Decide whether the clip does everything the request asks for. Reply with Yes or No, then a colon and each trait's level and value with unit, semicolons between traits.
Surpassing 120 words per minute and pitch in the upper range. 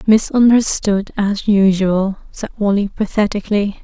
No: slow, 95 wpm; high, 205 Hz